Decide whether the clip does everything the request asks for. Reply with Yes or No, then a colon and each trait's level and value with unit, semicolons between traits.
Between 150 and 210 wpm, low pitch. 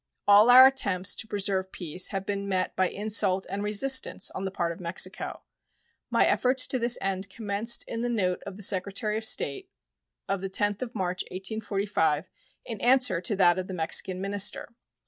No: average, 185 wpm; high, 200 Hz